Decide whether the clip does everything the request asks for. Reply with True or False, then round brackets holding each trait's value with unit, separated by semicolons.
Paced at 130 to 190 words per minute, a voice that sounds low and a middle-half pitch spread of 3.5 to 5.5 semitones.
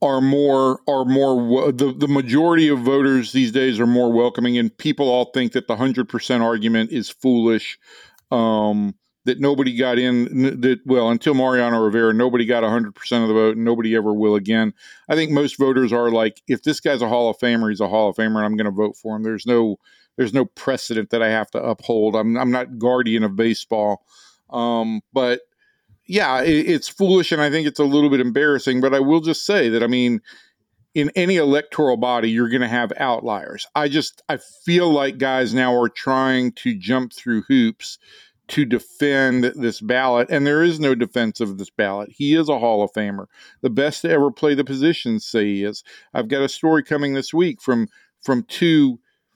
False (205 wpm; 125 Hz; 3.8 semitones)